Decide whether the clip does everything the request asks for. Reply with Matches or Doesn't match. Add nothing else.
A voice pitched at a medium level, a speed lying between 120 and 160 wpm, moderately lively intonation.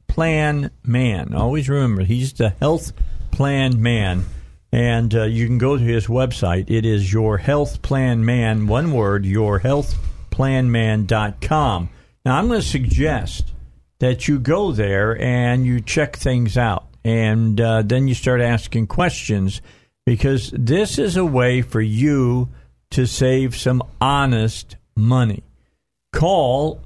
Doesn't match